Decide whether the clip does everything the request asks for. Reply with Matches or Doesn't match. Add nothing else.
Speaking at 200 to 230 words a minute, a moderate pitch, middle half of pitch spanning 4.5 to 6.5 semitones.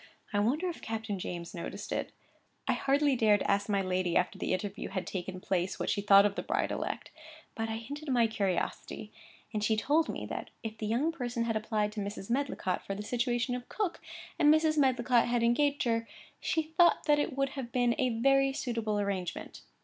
Doesn't match